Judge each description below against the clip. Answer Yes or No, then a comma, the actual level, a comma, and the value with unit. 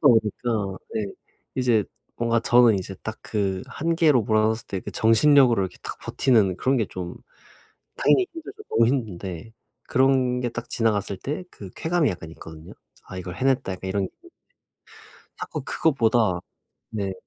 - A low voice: Yes, low, 115 Hz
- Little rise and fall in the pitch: No, average, 5.1 semitones